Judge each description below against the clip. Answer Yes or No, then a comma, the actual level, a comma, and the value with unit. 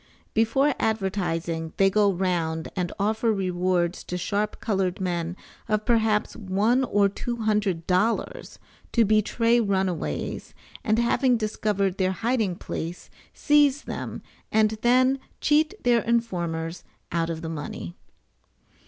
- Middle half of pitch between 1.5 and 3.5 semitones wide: No, average, 4.4 semitones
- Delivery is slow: Yes, slow, 125 wpm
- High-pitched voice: Yes, high, 200 Hz